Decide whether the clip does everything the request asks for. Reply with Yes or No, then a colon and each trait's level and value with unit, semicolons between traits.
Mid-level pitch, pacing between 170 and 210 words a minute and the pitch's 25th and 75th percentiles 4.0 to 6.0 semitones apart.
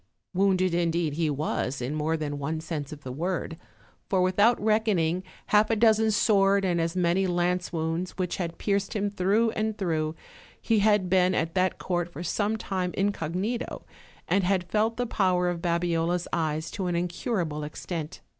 No: medium, 180 Hz; average, 175 wpm; average, 3.4 semitones